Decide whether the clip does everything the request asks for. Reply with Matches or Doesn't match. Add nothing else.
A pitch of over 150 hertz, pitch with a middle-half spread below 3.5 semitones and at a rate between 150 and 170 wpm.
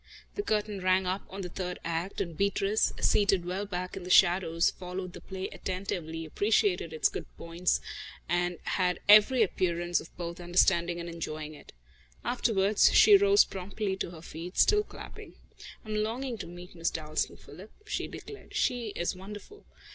Matches